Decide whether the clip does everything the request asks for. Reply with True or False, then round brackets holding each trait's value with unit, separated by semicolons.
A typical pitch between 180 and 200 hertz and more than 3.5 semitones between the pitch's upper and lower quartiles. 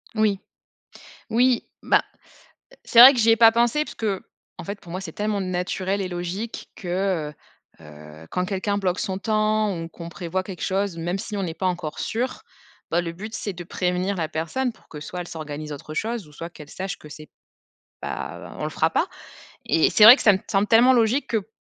True (190 Hz; 4.2 semitones)